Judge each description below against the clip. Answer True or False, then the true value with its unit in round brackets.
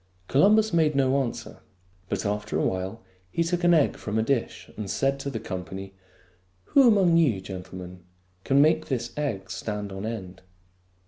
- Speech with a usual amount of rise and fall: False (7.8 semitones)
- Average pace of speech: True (175 wpm)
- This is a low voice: True (115 Hz)